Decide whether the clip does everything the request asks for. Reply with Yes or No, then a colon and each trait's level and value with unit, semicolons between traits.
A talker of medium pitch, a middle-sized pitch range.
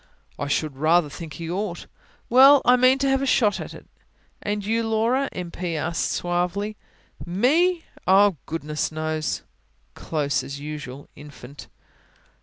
No: medium, 175 Hz; wide, 6.8 semitones